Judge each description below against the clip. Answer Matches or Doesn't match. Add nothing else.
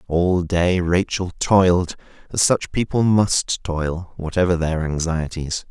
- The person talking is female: Doesn't match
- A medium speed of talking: Doesn't match